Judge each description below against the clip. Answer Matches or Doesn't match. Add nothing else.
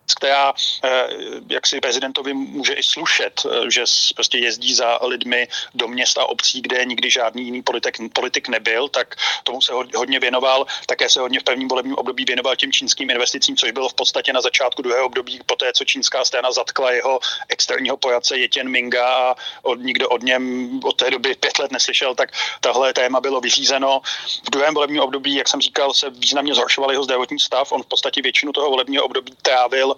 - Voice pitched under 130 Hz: Doesn't match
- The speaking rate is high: Matches